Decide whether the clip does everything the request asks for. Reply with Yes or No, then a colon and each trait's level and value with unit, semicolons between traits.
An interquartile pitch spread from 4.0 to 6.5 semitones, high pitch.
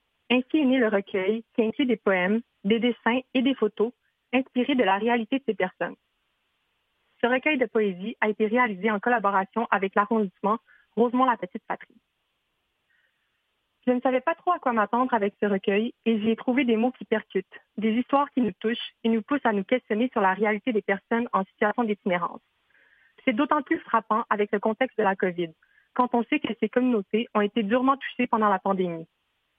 No: average, 3.1 semitones; high, 225 Hz